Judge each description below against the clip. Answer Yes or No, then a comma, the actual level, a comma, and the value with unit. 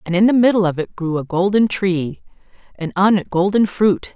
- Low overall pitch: No, high, 190 Hz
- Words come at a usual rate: No, fast, 215 wpm